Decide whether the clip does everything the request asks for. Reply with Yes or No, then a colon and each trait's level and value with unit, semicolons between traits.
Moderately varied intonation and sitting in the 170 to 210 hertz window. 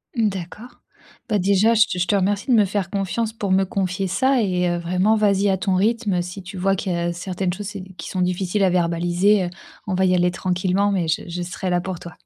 No: narrow, 2.2 semitones; high, 190 Hz